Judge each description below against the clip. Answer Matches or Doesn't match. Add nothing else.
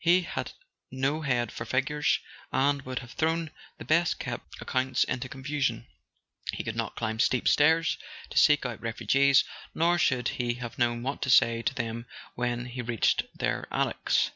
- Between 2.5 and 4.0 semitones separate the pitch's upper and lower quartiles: Matches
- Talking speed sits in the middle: Matches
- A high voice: Doesn't match